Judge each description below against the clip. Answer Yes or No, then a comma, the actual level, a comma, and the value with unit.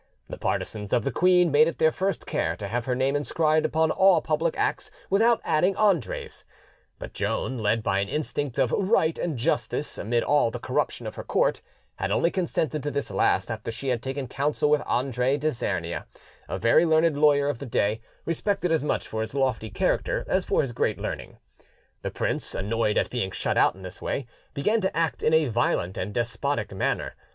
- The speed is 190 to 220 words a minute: Yes, average, 200 wpm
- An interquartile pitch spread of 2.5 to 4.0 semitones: No, wide, 5.6 semitones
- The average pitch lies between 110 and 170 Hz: Yes, medium, 140 Hz